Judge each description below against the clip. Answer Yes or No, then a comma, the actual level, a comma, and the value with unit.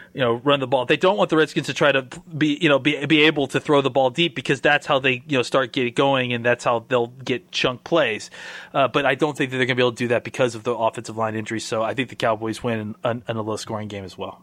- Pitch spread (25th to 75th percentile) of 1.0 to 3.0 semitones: No, average, 3.9 semitones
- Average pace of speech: No, fast, 305 wpm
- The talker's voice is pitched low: Yes, low, 130 Hz